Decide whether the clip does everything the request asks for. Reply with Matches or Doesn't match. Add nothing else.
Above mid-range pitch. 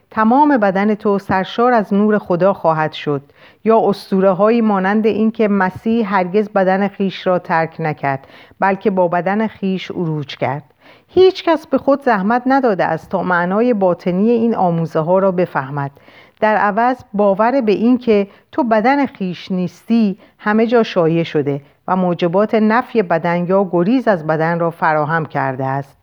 Matches